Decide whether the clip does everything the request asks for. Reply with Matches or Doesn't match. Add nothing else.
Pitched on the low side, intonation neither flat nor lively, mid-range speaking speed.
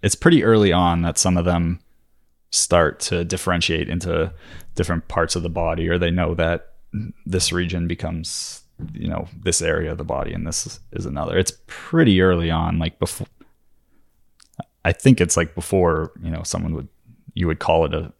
Doesn't match